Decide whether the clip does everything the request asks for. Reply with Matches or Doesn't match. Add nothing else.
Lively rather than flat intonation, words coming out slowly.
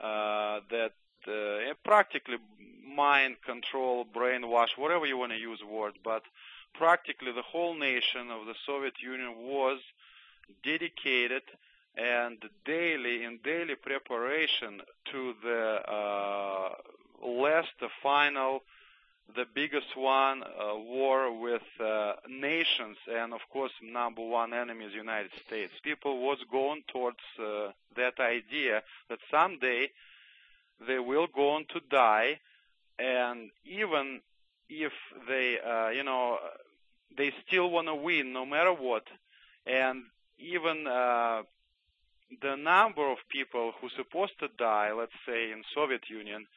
Doesn't match